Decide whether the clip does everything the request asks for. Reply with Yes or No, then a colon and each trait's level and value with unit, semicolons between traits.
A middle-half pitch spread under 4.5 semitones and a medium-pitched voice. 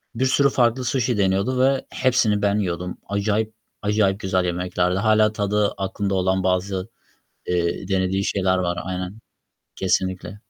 No: average, 2.7 semitones; low, 100 Hz